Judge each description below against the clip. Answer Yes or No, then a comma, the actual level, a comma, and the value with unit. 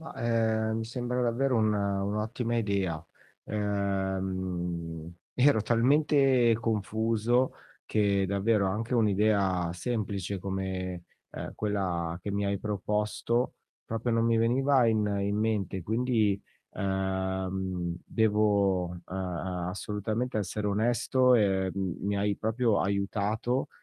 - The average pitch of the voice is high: No, low, 105 Hz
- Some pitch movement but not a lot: Yes, average, 3.0 semitones